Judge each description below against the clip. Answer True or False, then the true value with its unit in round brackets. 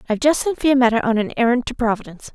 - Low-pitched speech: False (240 Hz)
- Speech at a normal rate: False (255 wpm)